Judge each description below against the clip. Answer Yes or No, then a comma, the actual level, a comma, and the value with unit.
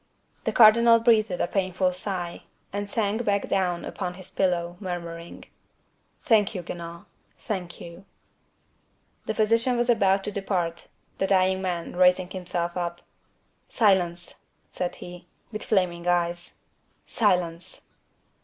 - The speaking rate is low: Yes, slow, 125 wpm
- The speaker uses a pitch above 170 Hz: Yes, medium, 185 Hz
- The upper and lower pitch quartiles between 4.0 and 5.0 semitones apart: No, average, 2.9 semitones